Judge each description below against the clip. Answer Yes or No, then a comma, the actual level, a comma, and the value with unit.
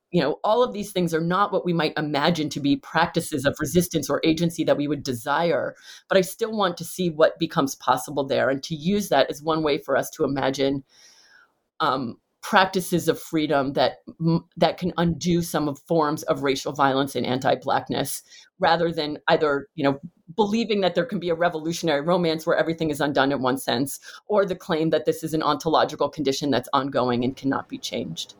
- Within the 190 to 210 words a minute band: Yes, average, 200 wpm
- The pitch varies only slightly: No, average, 3.4 semitones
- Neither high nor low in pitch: Yes, medium, 160 Hz